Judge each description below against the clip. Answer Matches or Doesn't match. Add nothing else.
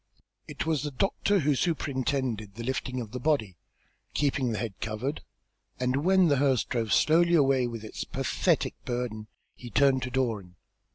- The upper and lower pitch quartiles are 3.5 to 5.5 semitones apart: Matches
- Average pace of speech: Matches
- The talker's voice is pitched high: Doesn't match